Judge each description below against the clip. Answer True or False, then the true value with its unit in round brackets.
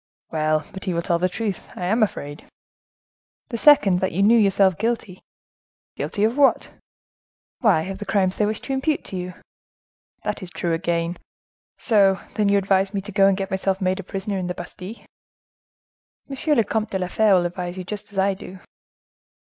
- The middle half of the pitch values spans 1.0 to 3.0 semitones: True (2.5 semitones)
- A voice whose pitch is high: True (195 Hz)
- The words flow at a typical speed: True (190 wpm)